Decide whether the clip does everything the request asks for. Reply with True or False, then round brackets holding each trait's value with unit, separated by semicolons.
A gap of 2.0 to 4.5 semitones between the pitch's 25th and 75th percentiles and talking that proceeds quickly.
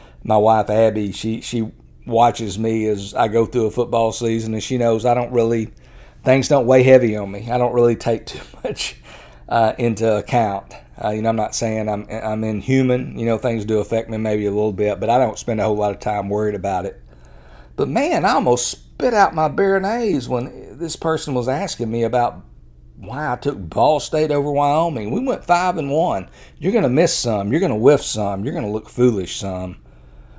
True (3.0 semitones; 210 wpm)